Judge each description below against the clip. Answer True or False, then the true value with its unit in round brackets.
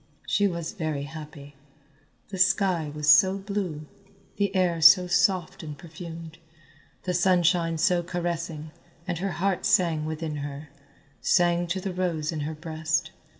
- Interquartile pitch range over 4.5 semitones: False (2.6 semitones)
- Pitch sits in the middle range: True (170 Hz)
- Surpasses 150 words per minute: False (145 wpm)